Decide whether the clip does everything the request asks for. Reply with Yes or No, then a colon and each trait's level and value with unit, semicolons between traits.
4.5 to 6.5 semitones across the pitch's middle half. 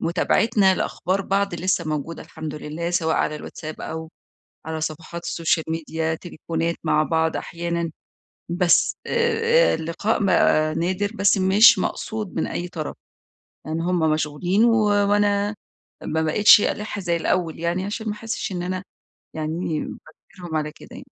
No: average, 3.8 semitones